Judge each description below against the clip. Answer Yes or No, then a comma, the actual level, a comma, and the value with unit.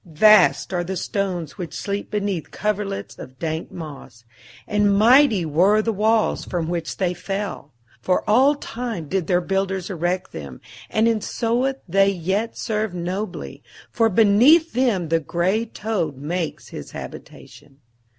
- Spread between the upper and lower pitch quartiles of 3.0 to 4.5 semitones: Yes, average, 4.0 semitones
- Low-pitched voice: No, high, 195 Hz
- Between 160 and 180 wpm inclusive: No, average, 145 wpm